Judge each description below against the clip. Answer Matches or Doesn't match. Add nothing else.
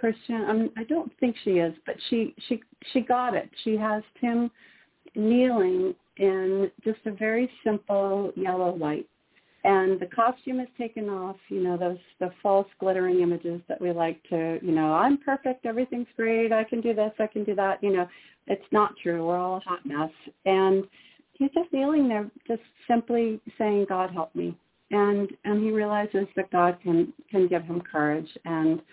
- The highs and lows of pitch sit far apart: Doesn't match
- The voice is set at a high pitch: Matches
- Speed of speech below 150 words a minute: Doesn't match